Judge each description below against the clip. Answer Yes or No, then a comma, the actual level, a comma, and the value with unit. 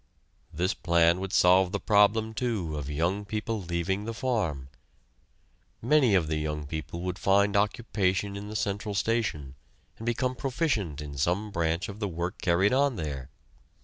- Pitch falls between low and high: No, very low, 95 Hz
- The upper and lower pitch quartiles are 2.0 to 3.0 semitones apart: No, average, 4.3 semitones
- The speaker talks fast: No, average, 160 wpm